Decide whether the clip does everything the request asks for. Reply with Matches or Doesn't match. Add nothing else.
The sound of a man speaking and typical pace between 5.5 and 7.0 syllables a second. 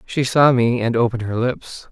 Doesn't match